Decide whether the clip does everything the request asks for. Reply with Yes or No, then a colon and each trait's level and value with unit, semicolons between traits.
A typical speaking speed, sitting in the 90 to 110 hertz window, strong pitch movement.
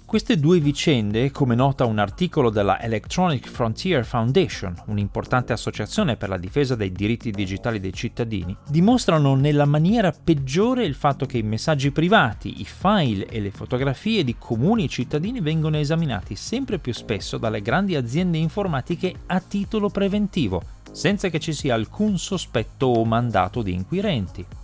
No: average, 150 wpm; medium, 140 Hz; wide, 8.3 semitones